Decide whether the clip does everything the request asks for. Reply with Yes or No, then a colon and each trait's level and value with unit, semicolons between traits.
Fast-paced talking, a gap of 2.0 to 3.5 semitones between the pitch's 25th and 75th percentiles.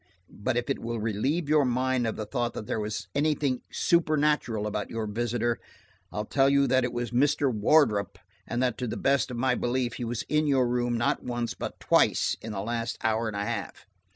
Yes: fast, 210 wpm; average, 3.2 semitones